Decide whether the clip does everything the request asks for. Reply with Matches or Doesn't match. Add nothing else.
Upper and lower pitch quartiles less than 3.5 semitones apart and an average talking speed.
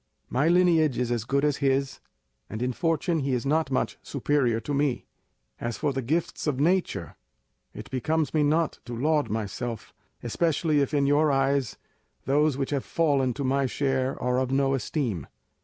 Matches